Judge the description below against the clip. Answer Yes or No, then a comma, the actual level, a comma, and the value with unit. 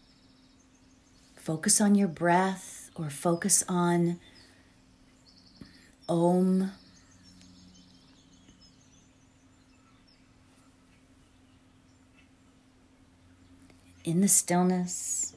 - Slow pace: Yes, slow, 45 wpm